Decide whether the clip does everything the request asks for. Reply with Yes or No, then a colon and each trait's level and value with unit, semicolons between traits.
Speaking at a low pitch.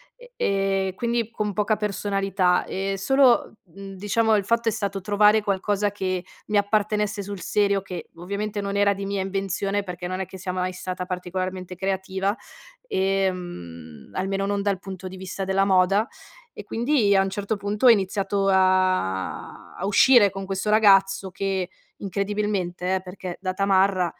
No: high, 195 Hz